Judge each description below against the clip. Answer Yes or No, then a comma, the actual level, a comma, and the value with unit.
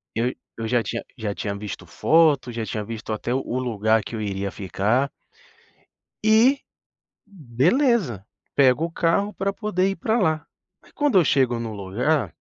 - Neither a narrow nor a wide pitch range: No, wide, 7.8 semitones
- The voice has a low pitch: Yes, low, 125 Hz